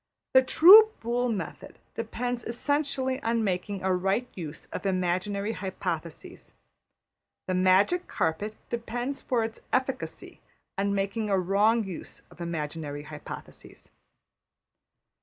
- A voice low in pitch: No, high, 205 Hz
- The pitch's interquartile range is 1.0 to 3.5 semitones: No, average, 4.9 semitones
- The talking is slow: Yes, slow, 115 wpm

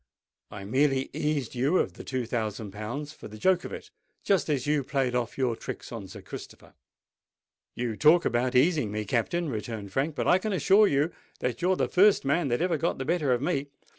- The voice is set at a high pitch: No, low, 135 Hz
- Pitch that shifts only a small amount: No, wide, 5.5 semitones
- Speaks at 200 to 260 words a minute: Yes, fast, 205 wpm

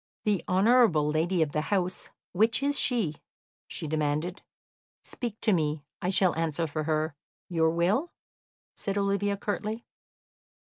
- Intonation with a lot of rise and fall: No, average, 4.8 semitones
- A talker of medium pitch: Yes, medium, 180 Hz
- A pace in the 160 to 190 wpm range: No, slow, 135 wpm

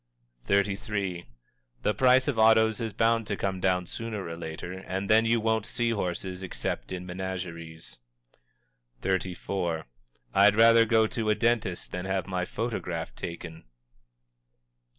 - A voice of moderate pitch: No, very low, 95 Hz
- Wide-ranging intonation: No, average, 3.7 semitones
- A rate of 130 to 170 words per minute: Yes, average, 140 wpm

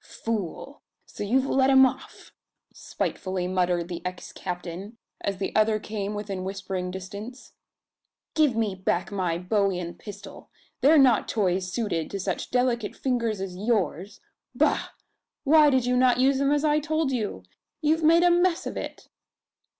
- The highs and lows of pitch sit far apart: Yes, wide, 5.9 semitones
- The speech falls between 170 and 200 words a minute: No, average, 160 wpm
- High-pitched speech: Yes, high, 215 Hz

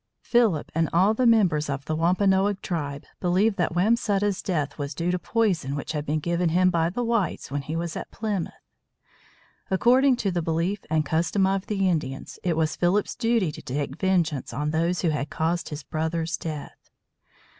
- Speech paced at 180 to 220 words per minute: Yes, average, 185 wpm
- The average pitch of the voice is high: No, medium, 170 Hz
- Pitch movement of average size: Yes, average, 4.0 semitones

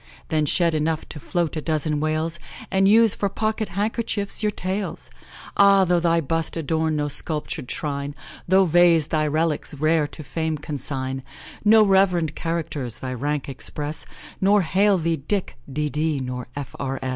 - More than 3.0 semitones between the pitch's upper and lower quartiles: Yes, average, 4.1 semitones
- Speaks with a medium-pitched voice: Yes, medium, 160 Hz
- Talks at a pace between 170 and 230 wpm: No, average, 155 wpm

